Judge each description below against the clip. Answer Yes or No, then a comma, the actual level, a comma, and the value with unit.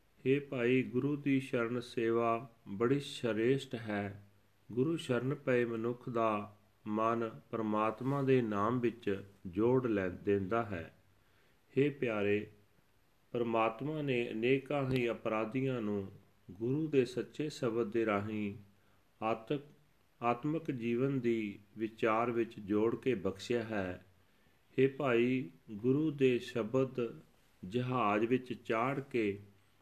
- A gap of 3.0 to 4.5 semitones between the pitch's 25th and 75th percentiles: Yes, average, 3.7 semitones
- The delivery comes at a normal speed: Yes, average, 110 wpm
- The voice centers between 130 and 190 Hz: No, low, 115 Hz